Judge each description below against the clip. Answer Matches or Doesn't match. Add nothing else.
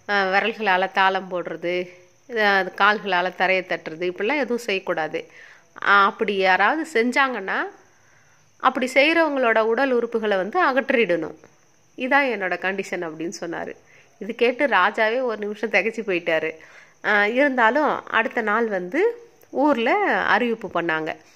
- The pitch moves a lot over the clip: Matches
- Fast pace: Doesn't match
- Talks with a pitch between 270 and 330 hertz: Doesn't match